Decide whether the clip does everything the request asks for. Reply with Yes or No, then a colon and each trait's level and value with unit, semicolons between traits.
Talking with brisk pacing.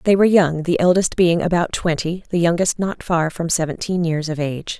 Yes: fast, 215 wpm